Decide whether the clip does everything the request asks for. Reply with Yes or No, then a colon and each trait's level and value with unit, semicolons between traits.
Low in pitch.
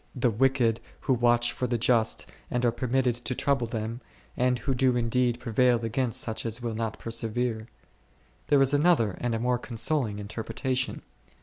Yes: low, 120 Hz